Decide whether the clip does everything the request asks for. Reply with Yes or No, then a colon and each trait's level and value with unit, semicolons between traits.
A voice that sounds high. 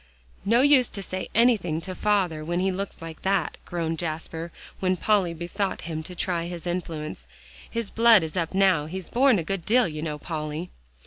No: medium, 180 Hz